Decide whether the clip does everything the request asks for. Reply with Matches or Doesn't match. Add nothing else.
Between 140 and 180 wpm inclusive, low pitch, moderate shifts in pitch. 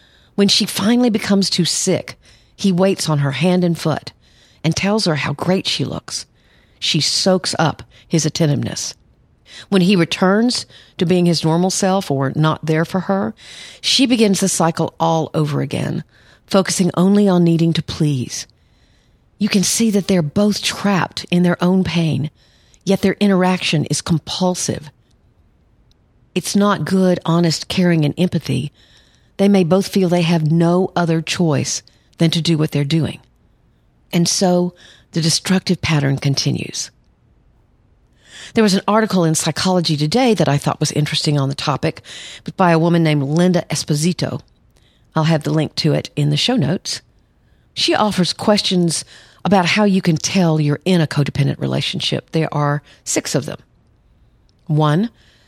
Doesn't match